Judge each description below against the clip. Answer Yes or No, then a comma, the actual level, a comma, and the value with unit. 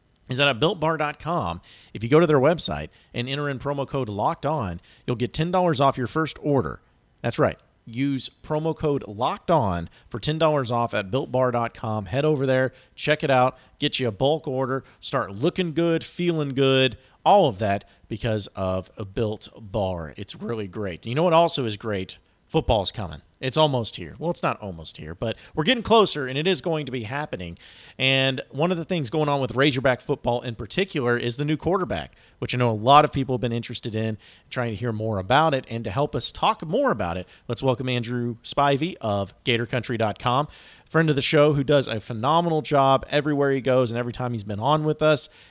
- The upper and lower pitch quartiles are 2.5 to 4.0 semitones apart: No, average, 4.8 semitones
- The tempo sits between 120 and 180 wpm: No, fast, 205 wpm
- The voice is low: Yes, low, 130 Hz